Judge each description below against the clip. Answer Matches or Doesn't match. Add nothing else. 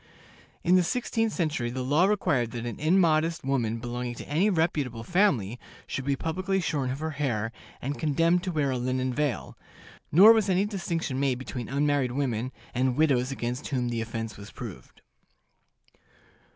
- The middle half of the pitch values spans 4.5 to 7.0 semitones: Matches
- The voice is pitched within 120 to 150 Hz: Matches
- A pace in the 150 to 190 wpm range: Matches